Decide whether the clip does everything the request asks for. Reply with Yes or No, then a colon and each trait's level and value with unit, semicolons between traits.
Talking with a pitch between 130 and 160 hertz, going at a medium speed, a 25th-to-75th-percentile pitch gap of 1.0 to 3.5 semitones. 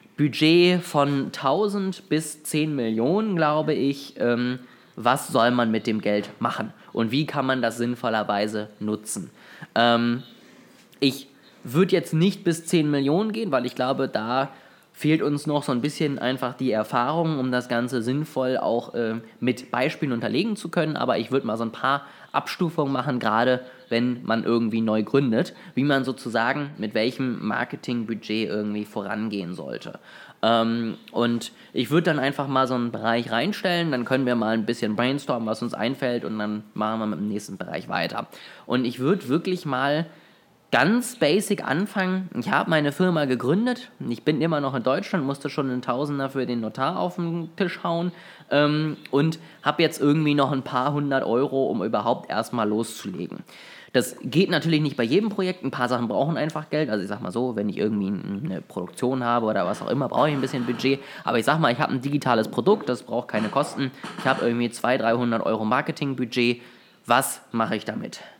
No: low, 135 Hz; average, 180 wpm; average, 4.6 semitones